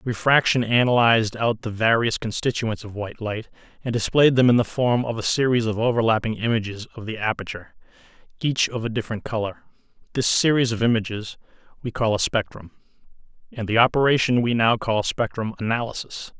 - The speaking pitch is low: Yes, low, 115 Hz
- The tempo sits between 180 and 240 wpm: No, average, 165 wpm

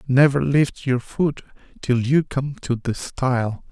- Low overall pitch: Yes, low, 130 Hz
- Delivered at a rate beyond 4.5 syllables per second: No, 3.9 syllables/s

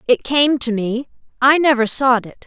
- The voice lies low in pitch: No, very high, 255 Hz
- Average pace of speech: Yes, average, 170 wpm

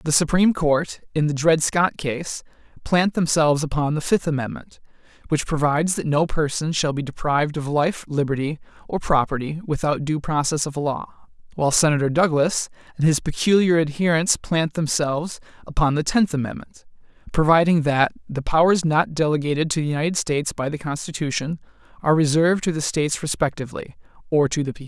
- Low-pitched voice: No, medium, 155 Hz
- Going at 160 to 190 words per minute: Yes, average, 165 wpm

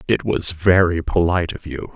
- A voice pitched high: No, very low, 90 Hz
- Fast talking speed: No, average, 185 wpm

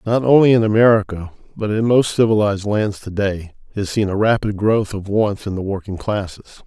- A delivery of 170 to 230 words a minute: Yes, average, 200 wpm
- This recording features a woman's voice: No, male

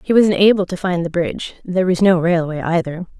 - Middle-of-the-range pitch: Yes, medium, 180 Hz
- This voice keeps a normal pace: No, fast, 225 wpm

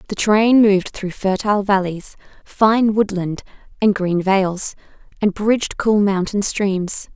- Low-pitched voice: No, high, 200 Hz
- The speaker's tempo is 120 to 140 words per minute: Yes, slow, 135 wpm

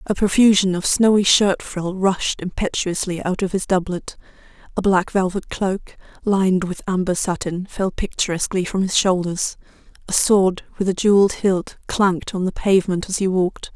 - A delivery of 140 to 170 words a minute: Yes, average, 165 wpm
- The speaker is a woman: Yes, female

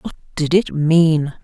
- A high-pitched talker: No, medium, 160 Hz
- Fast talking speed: No, average, 165 wpm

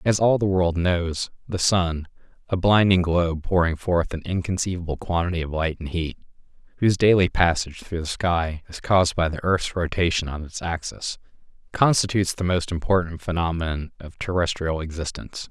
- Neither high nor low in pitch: No, very low, 85 Hz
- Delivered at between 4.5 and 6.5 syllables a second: Yes, 5.4 syllables/s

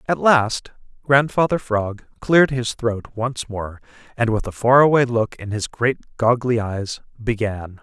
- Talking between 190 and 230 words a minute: No, average, 160 wpm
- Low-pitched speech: Yes, low, 115 Hz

